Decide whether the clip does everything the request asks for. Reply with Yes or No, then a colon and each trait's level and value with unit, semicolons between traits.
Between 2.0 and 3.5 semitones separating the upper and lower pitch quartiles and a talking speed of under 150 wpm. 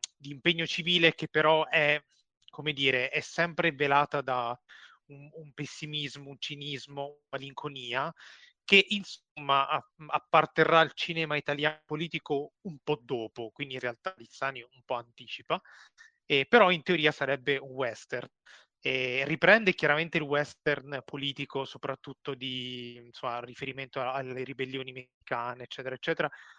Yes: average, 3.0 semitones; average, 130 wpm